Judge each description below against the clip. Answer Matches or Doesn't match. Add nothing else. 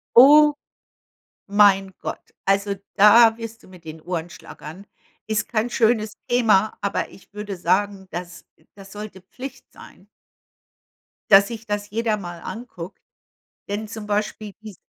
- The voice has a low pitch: Doesn't match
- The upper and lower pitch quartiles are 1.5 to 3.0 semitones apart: Matches